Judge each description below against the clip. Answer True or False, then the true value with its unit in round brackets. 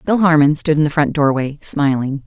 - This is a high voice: False (150 Hz)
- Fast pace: True (210 wpm)